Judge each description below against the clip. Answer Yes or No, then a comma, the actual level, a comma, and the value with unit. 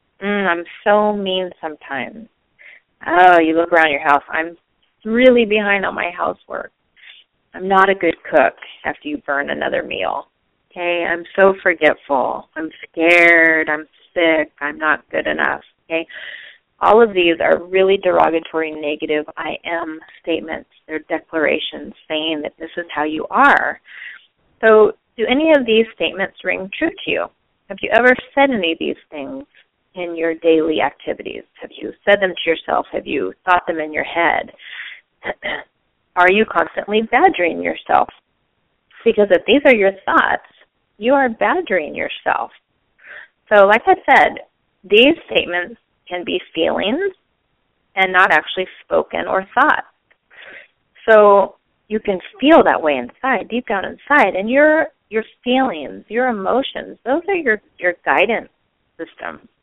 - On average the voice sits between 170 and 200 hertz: Yes, high, 190 Hz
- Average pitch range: No, wide, 6.0 semitones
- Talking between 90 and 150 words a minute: Yes, average, 145 wpm